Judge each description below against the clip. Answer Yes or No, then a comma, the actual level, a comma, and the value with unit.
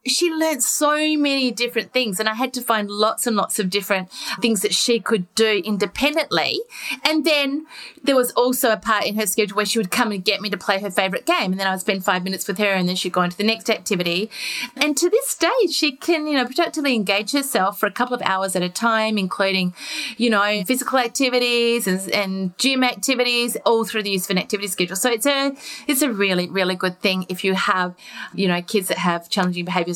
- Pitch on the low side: No, high, 220 Hz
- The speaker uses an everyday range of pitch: Yes, average, 4.9 semitones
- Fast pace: Yes, fast, 230 wpm